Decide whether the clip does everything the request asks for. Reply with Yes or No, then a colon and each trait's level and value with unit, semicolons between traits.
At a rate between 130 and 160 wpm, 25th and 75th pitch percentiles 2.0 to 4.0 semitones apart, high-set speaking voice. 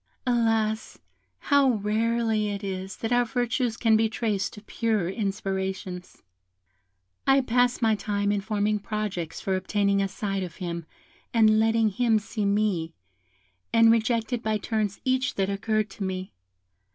Yes: average, 145 wpm; narrow, 2.5 semitones; high, 215 Hz